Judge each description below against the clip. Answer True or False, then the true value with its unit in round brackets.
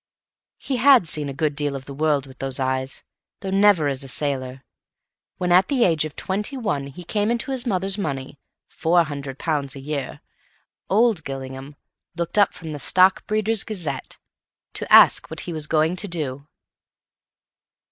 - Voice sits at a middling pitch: True (155 Hz)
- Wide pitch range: True (5.9 semitones)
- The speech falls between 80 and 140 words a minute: False (165 wpm)